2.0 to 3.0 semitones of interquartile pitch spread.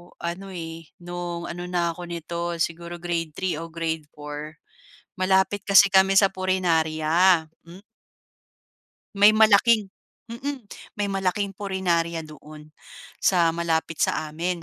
Yes: narrow, 2.6 semitones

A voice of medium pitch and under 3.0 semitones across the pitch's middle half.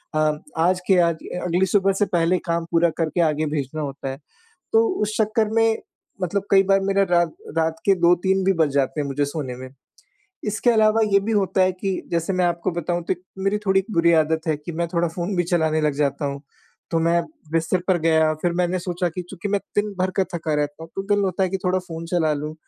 No: medium, 175 Hz; average, 3.3 semitones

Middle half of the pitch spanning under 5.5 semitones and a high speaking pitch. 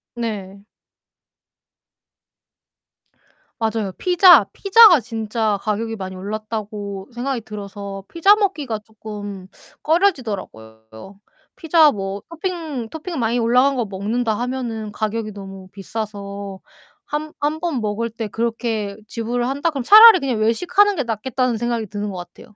Yes: average, 5.1 semitones; high, 225 Hz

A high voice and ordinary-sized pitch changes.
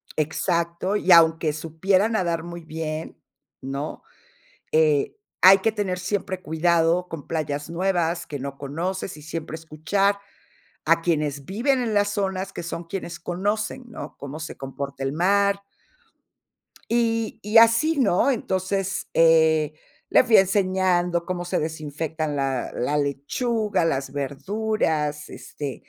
No: medium, 170 Hz; average, 4.2 semitones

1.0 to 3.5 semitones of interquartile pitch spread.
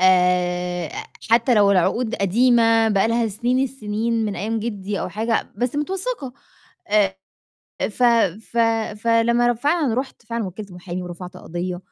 No: average, 4.1 semitones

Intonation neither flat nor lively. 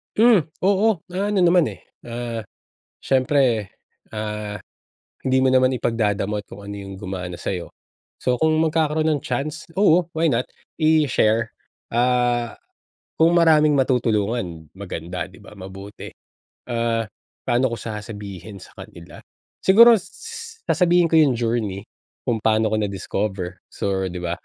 No: wide, 7.3 semitones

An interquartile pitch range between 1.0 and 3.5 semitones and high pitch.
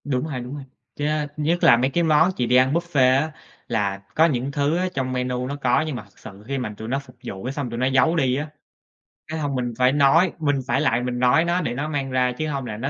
No: average, 3.2 semitones; low, 135 Hz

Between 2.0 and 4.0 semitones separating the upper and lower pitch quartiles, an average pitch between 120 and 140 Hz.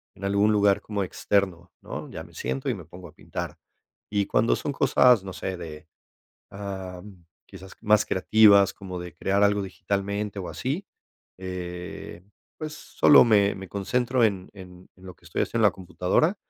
No: narrow, 2.4 semitones; low, 100 Hz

